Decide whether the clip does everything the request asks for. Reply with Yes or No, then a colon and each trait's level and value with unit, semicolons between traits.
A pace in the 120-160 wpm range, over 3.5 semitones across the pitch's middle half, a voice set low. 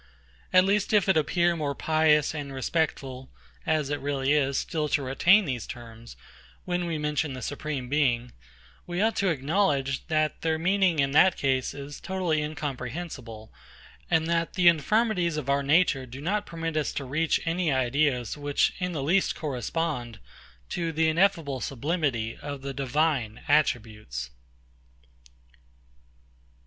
No: average, 145 wpm; average, 3.9 semitones; medium, 150 Hz